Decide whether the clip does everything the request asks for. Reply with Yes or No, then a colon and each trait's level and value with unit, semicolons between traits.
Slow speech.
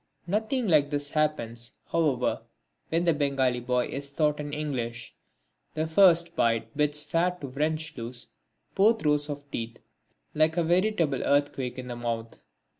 No: average, 150 wpm